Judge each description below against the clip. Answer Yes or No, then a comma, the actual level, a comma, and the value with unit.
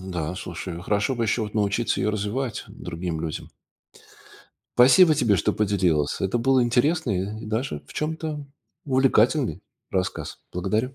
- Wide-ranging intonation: Yes, wide, 5.9 semitones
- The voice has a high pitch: No, low, 110 Hz